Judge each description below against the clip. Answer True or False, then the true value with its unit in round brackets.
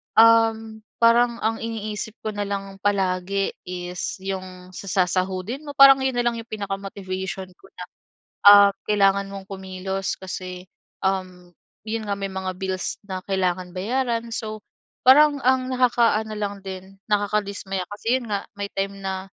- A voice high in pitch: True (200 Hz)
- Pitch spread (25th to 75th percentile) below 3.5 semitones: True (2.9 semitones)